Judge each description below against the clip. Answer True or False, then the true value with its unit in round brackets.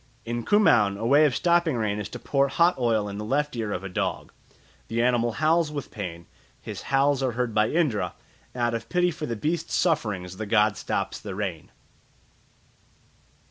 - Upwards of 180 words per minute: True (190 wpm)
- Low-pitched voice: True (120 Hz)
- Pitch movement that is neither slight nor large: False (6.1 semitones)